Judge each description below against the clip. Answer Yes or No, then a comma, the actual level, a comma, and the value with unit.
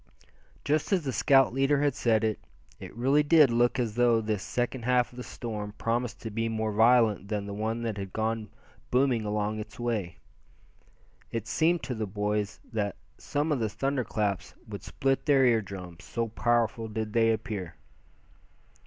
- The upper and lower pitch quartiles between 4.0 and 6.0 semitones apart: No, average, 2.9 semitones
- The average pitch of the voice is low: Yes, low, 115 Hz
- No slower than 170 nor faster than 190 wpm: Yes, average, 180 wpm